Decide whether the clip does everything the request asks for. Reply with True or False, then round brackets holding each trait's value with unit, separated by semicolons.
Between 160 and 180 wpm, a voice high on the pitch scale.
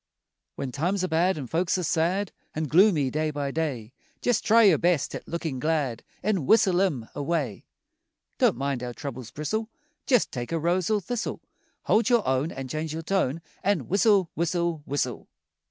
False (175 wpm; 160 Hz)